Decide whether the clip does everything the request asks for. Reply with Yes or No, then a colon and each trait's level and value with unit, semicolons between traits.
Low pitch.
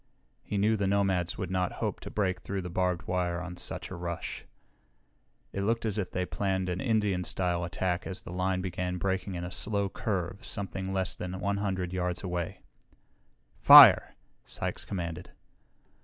Yes: very low, 95 Hz